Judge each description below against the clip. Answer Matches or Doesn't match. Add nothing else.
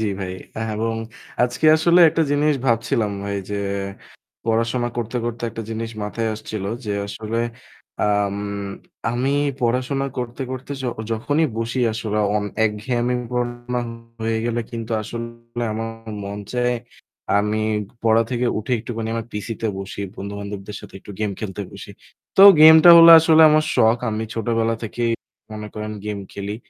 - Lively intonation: Doesn't match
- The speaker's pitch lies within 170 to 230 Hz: Doesn't match